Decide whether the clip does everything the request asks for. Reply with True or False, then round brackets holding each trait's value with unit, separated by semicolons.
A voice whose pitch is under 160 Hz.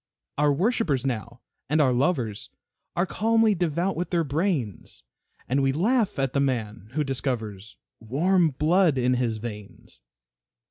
True (140 Hz)